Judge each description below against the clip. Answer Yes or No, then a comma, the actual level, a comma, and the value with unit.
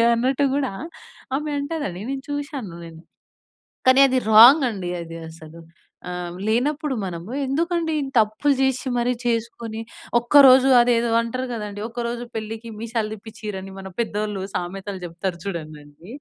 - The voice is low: No, high, 230 Hz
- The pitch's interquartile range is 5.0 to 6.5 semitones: Yes, wide, 5.4 semitones